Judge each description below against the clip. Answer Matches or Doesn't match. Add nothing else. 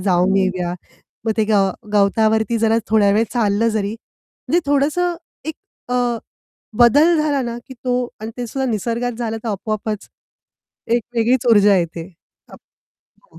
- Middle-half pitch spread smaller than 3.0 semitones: Doesn't match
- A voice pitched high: Matches